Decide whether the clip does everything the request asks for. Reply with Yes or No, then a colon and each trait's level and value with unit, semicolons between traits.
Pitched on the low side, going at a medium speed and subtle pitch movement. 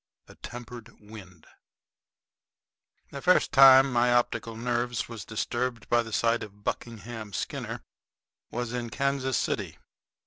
No: low, 120 Hz; slow, 125 wpm; narrow, 1.7 semitones